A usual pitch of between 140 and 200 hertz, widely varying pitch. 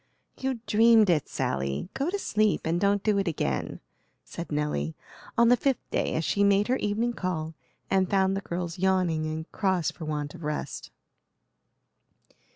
No: medium, 185 Hz; average, 4.9 semitones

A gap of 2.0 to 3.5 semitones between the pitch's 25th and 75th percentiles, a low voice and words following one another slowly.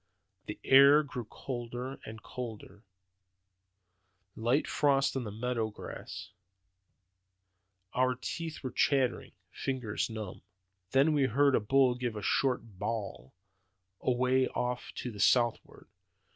Yes: average, 3.2 semitones; low, 125 Hz; slow, 115 wpm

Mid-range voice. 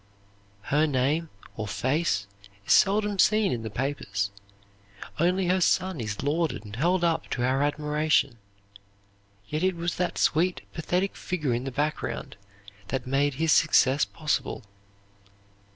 Yes: medium, 150 Hz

